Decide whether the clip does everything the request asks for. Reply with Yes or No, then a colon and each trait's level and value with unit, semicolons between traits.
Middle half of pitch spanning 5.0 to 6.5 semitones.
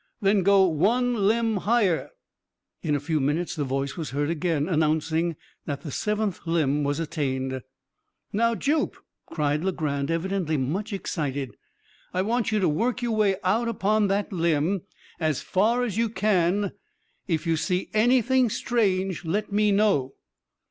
Yes: wide, 5.6 semitones